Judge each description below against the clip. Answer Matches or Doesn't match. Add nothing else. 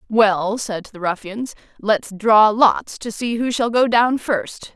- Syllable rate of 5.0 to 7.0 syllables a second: Doesn't match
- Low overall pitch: Doesn't match